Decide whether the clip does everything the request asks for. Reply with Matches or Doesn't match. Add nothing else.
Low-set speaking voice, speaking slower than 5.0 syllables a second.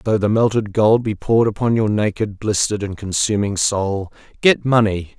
Doesn't match